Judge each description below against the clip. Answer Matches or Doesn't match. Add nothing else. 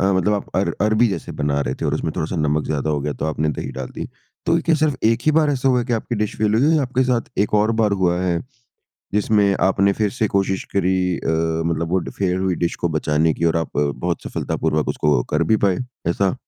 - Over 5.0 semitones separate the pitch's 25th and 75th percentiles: Matches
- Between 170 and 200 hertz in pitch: Doesn't match